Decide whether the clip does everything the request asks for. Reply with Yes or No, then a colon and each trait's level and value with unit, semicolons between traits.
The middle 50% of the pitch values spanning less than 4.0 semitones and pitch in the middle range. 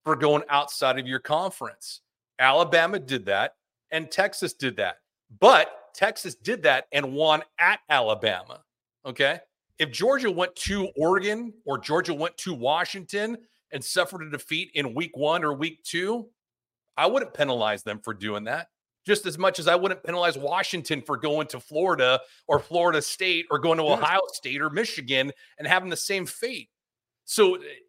No: average, 4.7 semitones; medium, 165 Hz